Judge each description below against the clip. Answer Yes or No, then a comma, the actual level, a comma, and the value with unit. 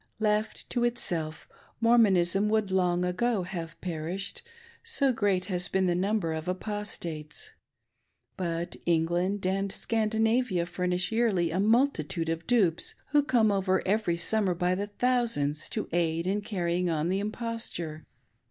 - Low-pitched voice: No, high, 190 Hz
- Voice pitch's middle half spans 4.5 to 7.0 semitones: No, average, 4.1 semitones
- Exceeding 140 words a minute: No, slow, 135 wpm